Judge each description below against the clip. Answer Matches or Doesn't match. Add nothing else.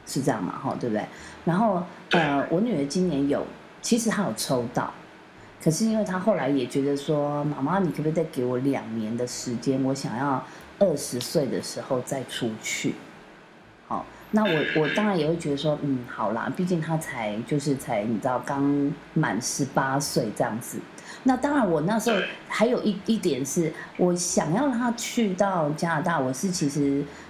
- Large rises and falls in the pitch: Matches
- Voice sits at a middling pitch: Matches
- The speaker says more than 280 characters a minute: Doesn't match